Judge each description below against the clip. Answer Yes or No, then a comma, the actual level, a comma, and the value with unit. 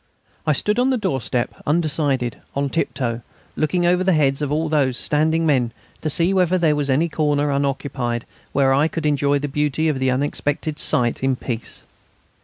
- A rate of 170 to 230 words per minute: Yes, average, 185 wpm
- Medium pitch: Yes, medium, 145 Hz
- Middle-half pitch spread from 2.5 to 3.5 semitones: Yes, average, 3.0 semitones